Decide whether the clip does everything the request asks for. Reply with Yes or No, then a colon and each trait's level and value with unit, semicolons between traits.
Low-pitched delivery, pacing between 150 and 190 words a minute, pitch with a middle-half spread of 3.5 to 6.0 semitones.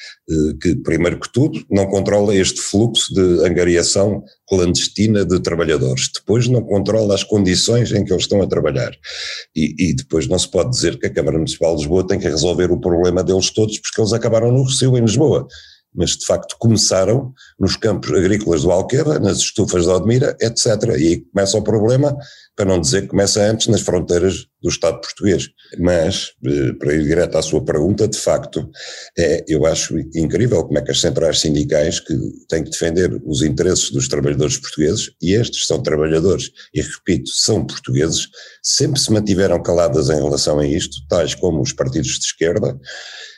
Yes: low, 100 Hz; fast, 185 wpm; average, 3.9 semitones